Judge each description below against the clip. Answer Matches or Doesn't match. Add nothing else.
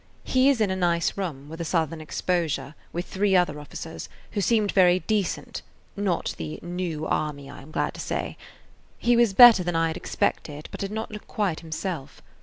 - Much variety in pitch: Doesn't match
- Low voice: Doesn't match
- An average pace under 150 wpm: Doesn't match